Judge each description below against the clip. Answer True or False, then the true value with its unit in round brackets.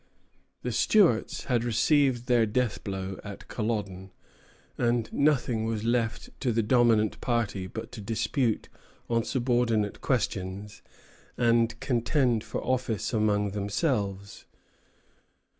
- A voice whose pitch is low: True (115 Hz)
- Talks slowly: True (110 wpm)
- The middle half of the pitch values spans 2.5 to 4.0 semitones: True (2.8 semitones)